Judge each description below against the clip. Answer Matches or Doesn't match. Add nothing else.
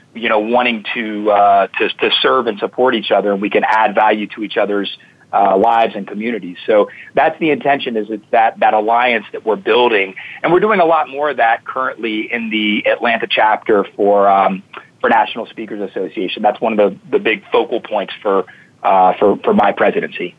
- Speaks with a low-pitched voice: Matches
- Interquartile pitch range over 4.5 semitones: Matches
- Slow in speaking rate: Doesn't match